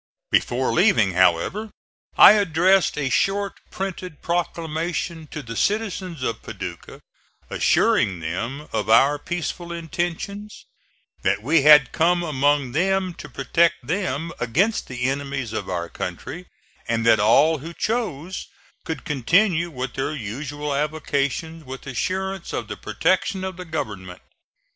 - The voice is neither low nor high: Yes, medium, 155 Hz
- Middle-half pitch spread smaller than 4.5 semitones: No, wide, 5.6 semitones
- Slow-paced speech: Yes, slow, 130 wpm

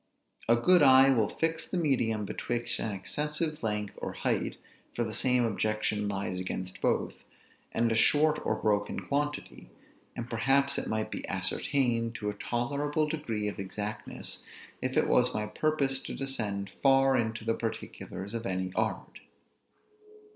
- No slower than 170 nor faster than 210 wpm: No, average, 155 wpm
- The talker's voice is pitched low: Yes, low, 115 Hz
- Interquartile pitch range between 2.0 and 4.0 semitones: No, average, 4.8 semitones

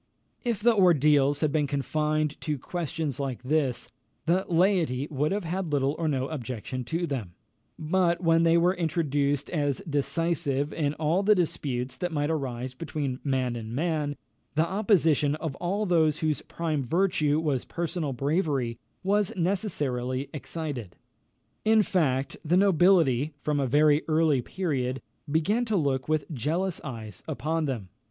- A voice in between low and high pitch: Yes, medium, 150 Hz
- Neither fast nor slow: Yes, average, 150 wpm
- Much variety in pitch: No, average, 3.8 semitones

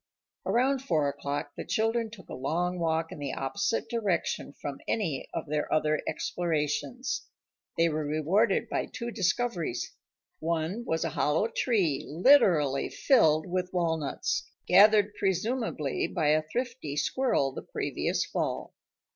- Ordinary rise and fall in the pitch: No, wide, 6.3 semitones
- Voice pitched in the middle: Yes, medium, 170 Hz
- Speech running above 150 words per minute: No, slow, 135 wpm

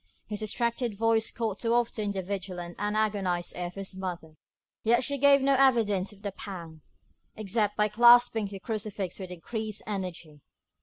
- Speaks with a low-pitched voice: No, high, 210 Hz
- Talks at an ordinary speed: Yes, average, 165 wpm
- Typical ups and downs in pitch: Yes, average, 3.4 semitones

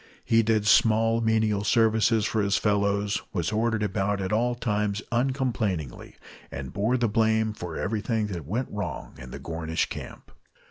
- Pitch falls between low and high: No, low, 105 Hz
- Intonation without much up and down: Yes, narrow, 2.2 semitones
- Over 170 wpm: No, average, 155 wpm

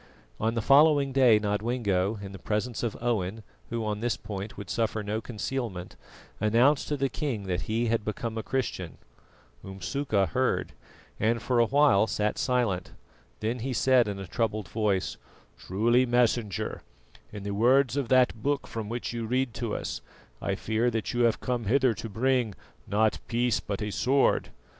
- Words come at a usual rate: Yes, average, 170 wpm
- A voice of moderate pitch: No, low, 115 Hz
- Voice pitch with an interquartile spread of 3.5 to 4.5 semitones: No, average, 3.1 semitones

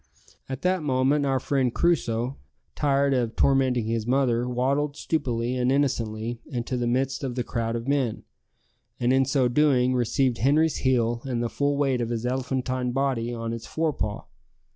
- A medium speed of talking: Yes, average, 170 wpm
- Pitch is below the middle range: Yes, low, 130 Hz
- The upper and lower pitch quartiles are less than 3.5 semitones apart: Yes, narrow, 2.5 semitones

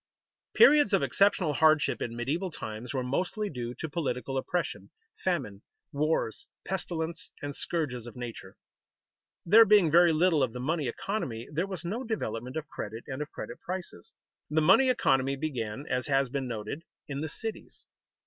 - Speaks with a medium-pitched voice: Yes, medium, 150 Hz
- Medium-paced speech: Yes, average, 165 wpm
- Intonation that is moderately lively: No, wide, 5.8 semitones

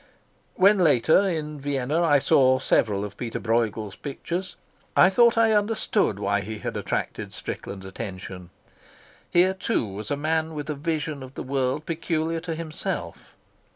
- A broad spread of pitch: Yes, wide, 6.7 semitones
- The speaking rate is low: No, average, 155 wpm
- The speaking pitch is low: No, medium, 150 Hz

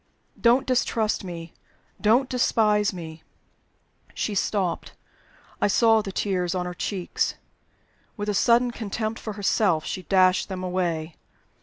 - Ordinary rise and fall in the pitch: Yes, average, 3.6 semitones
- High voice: Yes, high, 200 Hz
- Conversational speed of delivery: No, slow, 130 wpm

